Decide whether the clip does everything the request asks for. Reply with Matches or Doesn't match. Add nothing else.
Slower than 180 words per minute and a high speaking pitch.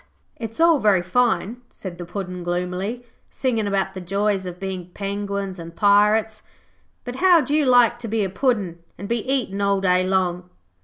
Matches